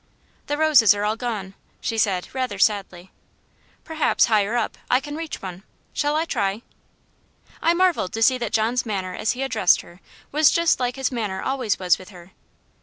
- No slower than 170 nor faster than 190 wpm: Yes, average, 180 wpm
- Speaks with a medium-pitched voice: No, high, 225 Hz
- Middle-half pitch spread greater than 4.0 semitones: Yes, wide, 5.5 semitones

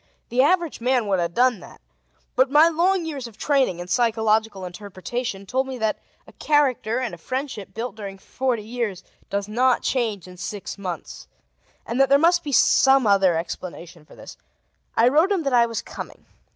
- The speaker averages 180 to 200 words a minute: Yes, average, 185 wpm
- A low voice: No, high, 235 Hz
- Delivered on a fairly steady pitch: No, average, 5.1 semitones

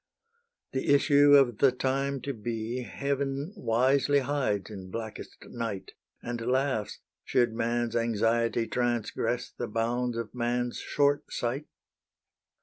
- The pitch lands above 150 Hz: No, low, 120 Hz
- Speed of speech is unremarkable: No, slow, 120 wpm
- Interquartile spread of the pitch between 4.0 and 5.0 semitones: No, average, 3.2 semitones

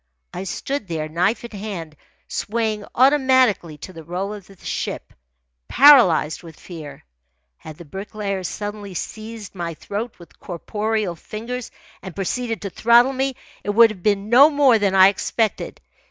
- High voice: Yes, high, 205 Hz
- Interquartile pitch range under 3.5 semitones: No, average, 4.6 semitones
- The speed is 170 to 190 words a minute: No, average, 155 wpm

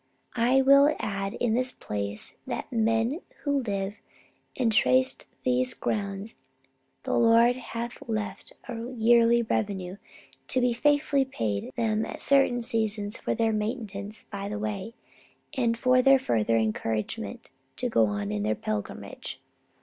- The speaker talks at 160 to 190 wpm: No, average, 145 wpm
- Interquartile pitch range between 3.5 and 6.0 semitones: Yes, average, 4.0 semitones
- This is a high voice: Yes, high, 220 Hz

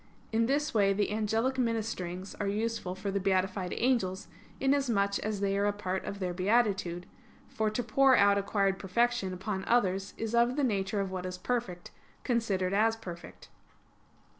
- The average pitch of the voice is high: Yes, high, 200 Hz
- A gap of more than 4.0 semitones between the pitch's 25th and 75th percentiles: No, average, 3.3 semitones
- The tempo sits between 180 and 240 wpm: No, average, 165 wpm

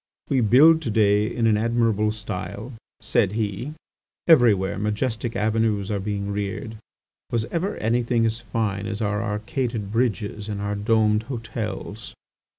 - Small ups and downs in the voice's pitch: Yes, narrow, 2.1 semitones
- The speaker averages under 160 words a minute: Yes, average, 140 wpm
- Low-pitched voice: Yes, low, 110 Hz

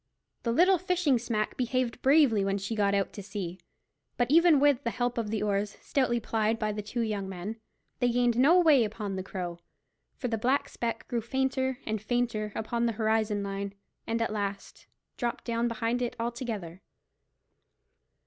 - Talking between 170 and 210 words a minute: Yes, average, 175 wpm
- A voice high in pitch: Yes, high, 230 Hz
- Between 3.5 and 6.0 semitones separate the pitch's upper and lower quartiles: No, average, 2.9 semitones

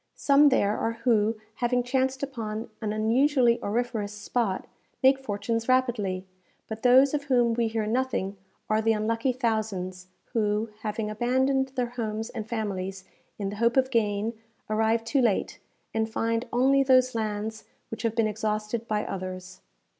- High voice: Yes, high, 225 Hz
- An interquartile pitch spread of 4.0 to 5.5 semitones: No, average, 2.8 semitones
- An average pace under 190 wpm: Yes, average, 155 wpm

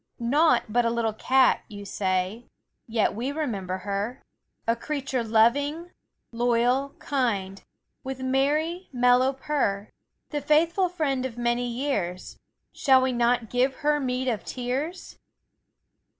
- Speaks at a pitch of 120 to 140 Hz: No, very high, 250 Hz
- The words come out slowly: Yes, slow, 125 wpm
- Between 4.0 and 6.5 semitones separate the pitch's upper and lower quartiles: No, average, 3.5 semitones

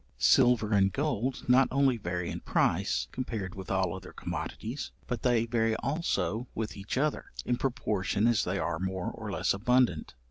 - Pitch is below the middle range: Yes, low, 115 Hz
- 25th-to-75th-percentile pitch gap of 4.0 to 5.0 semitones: Yes, average, 4.5 semitones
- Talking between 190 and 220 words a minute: No, average, 170 wpm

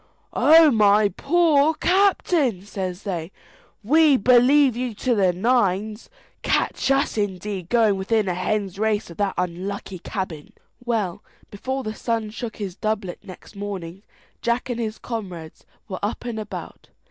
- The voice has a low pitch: No, high, 215 Hz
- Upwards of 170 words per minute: No, average, 145 wpm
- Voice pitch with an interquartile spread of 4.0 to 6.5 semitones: Yes, average, 4.3 semitones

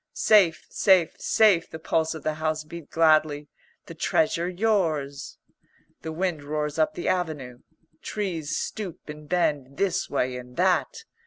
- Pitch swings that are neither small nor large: Yes, average, 3.2 semitones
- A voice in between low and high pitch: Yes, medium, 160 Hz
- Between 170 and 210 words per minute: No, average, 145 wpm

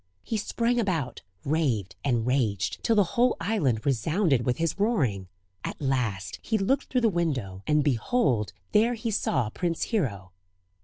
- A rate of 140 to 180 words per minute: Yes, average, 155 wpm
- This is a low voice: No, medium, 150 Hz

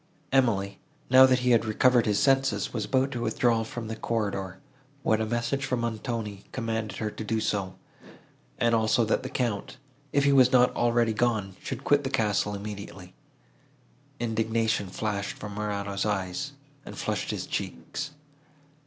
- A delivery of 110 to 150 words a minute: No, average, 160 wpm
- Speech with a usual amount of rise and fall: Yes, average, 3.2 semitones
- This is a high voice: No, low, 115 Hz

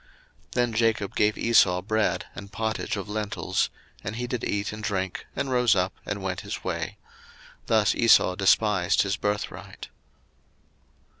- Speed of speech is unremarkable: Yes, average, 150 wpm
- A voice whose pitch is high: No, low, 105 Hz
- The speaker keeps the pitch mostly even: Yes, narrow, 2.3 semitones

